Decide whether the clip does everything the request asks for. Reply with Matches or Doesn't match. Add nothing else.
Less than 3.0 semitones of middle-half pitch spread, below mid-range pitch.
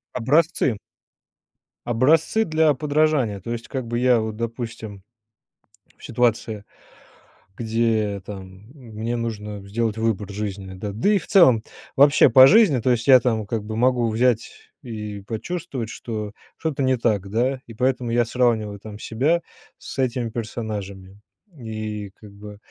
Doesn't match